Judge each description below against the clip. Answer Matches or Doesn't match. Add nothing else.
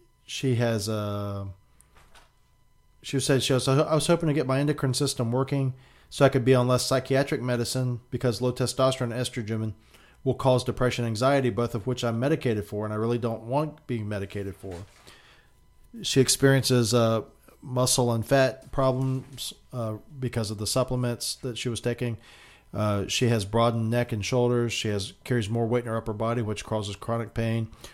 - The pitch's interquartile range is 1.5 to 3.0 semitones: Matches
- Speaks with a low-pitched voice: Matches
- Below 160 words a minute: Doesn't match